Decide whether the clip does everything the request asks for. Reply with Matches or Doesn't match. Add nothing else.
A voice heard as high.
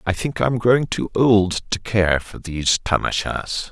Doesn't match